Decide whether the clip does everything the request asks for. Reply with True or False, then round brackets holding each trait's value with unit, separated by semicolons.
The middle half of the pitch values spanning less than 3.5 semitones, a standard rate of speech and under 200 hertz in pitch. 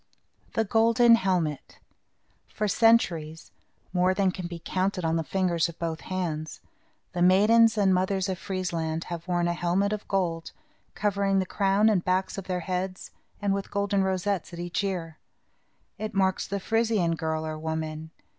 True (2.9 semitones; 165 wpm; 185 Hz)